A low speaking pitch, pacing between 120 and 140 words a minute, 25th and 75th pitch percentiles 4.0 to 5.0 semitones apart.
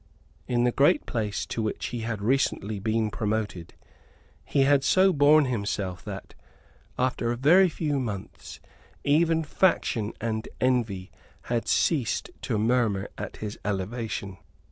Yes: low, 115 Hz; slow, 135 wpm; average, 4.7 semitones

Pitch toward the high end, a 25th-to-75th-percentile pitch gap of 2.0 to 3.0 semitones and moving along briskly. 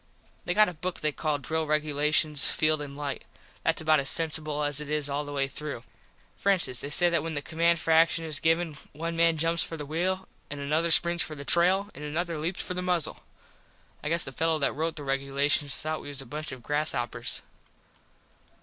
No: medium, 155 Hz; narrow, 2.5 semitones; fast, 220 wpm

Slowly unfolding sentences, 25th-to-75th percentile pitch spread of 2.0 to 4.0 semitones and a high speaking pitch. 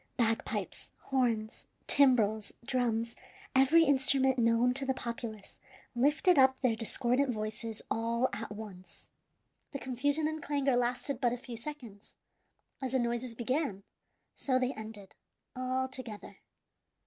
Yes: slow, 125 wpm; average, 2.8 semitones; high, 245 Hz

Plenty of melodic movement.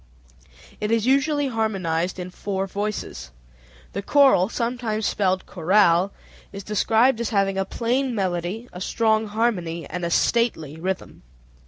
No: average, 4.0 semitones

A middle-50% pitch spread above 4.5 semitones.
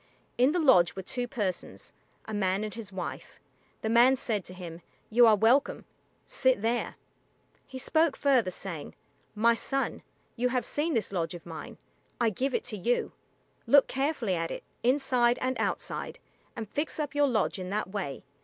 Yes: average, 5.3 semitones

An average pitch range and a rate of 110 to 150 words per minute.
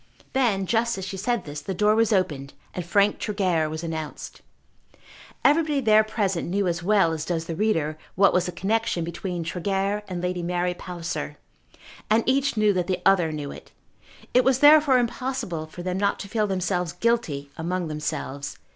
No: average, 4.2 semitones; average, 180 wpm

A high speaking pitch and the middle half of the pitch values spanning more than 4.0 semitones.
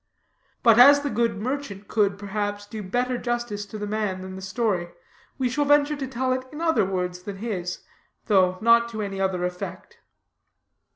Yes: high, 215 Hz; average, 4.4 semitones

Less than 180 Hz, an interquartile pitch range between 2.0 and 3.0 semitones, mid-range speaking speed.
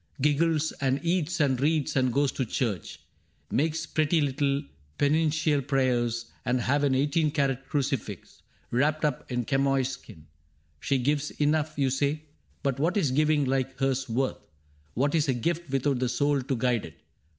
Yes: medium, 140 Hz; narrow, 2.6 semitones; average, 160 wpm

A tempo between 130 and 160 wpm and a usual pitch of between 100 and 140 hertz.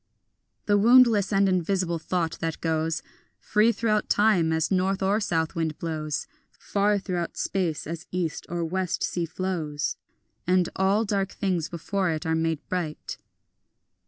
No: average, 145 wpm; medium, 180 Hz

